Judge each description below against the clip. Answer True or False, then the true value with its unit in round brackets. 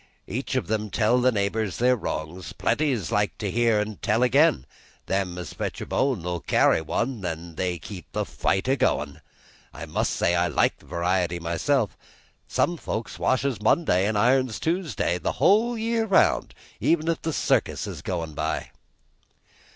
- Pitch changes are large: True (6.8 semitones)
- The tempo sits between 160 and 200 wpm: True (165 wpm)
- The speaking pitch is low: True (105 Hz)